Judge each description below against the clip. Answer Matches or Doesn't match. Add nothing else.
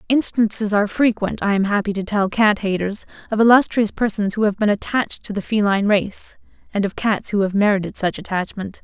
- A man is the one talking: Doesn't match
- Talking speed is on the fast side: Doesn't match